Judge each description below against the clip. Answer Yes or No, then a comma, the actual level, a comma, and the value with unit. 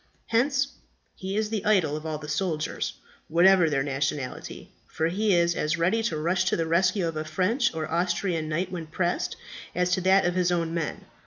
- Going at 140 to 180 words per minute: No, average, 195 wpm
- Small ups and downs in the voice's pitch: No, average, 3.2 semitones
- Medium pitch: Yes, medium, 175 Hz